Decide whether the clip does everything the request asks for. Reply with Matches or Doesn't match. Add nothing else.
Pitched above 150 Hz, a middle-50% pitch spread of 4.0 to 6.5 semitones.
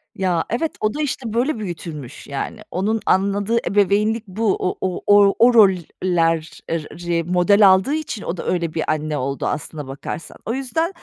Matches